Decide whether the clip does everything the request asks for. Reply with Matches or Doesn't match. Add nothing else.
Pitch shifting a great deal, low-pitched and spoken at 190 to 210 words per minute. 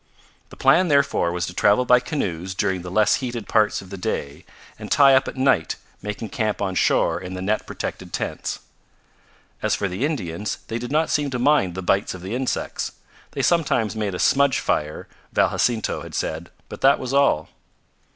Matches